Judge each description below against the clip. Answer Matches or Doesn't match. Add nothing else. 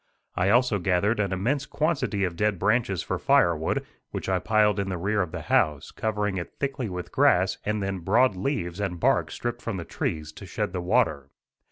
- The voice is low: Matches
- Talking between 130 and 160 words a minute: Doesn't match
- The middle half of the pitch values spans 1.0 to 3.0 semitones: Doesn't match